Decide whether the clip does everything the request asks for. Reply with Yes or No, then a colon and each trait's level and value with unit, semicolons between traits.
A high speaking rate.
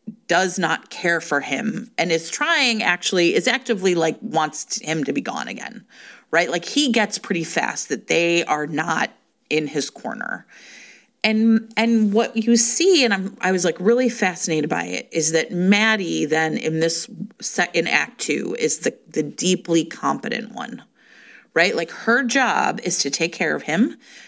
No: average, 175 wpm